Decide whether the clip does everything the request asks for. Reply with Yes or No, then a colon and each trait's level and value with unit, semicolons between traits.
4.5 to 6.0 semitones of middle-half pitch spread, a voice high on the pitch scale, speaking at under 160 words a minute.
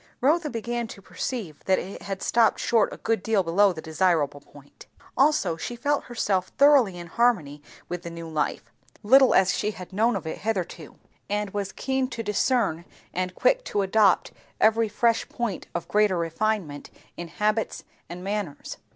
No: average, 5.0 semitones; high, 205 Hz; average, 170 wpm